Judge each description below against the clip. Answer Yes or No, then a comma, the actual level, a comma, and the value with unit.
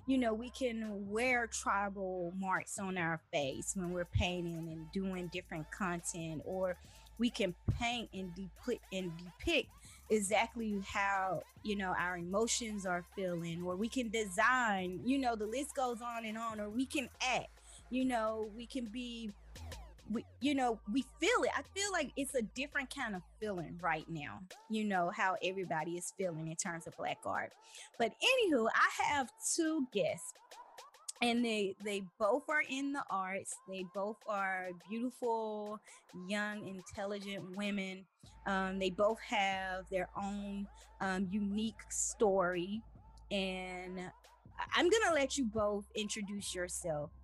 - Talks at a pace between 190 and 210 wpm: No, average, 155 wpm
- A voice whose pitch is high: Yes, high, 205 Hz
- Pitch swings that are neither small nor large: Yes, average, 4.3 semitones